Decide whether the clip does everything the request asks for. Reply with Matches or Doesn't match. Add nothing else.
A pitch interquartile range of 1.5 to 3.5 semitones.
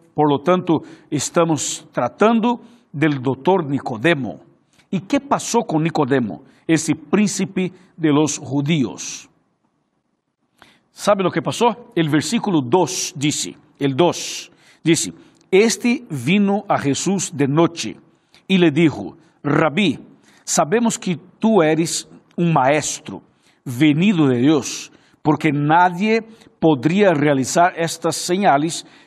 Doesn't match